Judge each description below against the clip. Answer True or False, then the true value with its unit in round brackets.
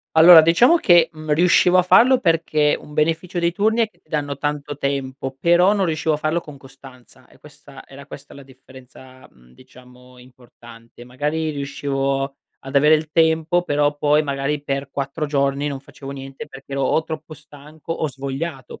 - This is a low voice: False (145 Hz)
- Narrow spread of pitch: False (3.0 semitones)